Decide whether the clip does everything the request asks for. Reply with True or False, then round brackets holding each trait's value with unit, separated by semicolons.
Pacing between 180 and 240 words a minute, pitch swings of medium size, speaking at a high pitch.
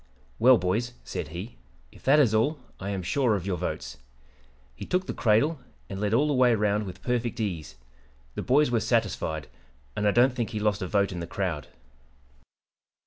False (195 wpm; 4.6 semitones; 105 Hz)